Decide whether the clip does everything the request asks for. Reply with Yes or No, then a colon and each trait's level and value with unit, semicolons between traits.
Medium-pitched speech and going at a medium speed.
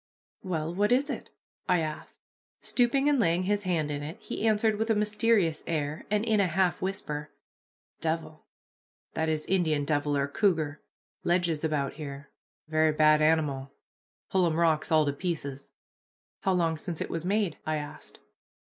Yes: medium, 165 Hz; average, 165 wpm